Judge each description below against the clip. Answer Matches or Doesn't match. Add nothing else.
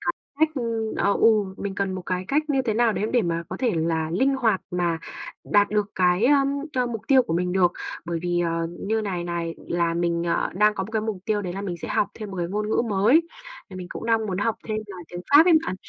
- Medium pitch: Doesn't match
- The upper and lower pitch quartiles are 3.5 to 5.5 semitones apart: Matches